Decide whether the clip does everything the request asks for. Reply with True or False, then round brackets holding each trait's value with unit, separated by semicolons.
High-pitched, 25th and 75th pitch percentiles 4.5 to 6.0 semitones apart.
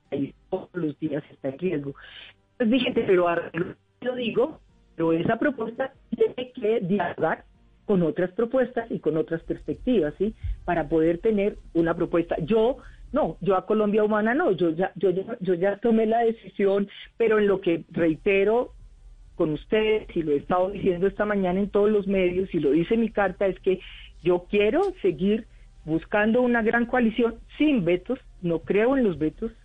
True (200 Hz; 5.1 semitones)